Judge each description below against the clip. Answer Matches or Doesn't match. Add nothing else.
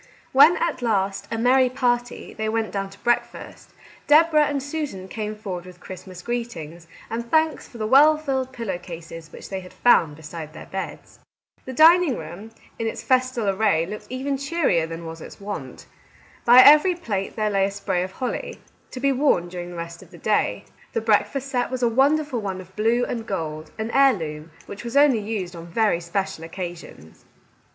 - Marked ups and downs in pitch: Matches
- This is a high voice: Matches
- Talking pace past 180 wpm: Matches